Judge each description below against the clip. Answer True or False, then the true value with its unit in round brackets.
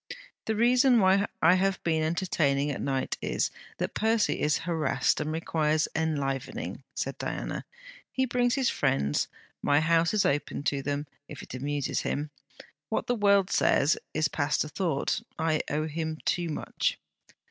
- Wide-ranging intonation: False (4.8 semitones)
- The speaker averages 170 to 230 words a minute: False (160 wpm)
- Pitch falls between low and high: True (160 Hz)